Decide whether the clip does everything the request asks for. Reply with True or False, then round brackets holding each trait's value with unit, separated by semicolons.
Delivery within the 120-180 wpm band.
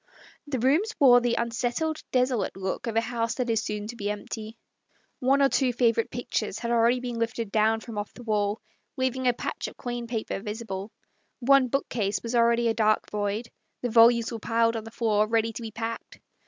False (205 wpm)